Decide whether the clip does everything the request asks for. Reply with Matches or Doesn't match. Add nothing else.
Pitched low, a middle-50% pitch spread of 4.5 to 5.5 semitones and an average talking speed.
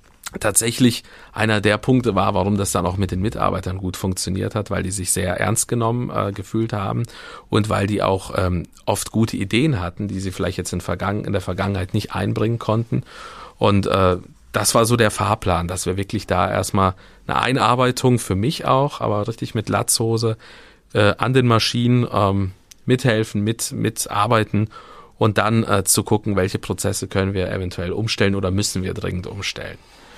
Doesn't match